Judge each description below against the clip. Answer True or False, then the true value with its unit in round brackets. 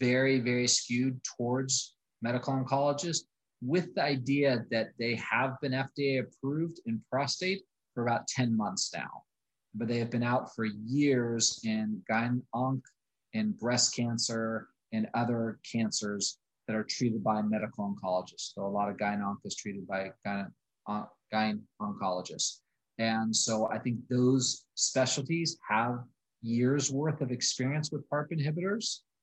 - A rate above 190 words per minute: False (145 wpm)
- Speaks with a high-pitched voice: False (125 Hz)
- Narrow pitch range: False (3.6 semitones)